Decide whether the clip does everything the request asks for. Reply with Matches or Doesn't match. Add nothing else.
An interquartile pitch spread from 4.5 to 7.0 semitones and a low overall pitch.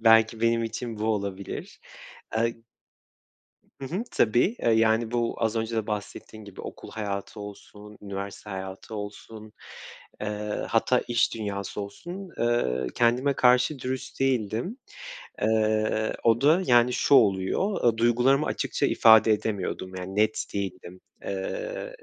Doesn't match